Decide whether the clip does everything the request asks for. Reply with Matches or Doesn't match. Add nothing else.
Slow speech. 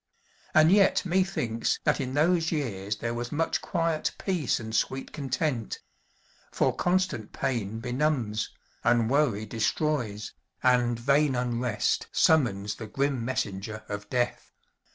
Matches